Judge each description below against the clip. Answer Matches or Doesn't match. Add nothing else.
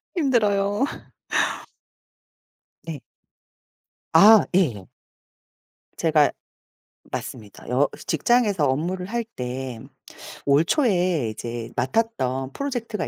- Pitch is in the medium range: Matches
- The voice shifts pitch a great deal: Matches